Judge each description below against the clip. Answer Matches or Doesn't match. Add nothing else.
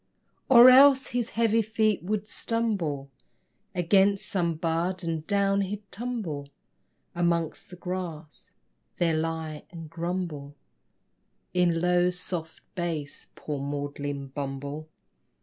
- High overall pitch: Doesn't match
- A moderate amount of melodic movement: Matches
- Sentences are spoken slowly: Matches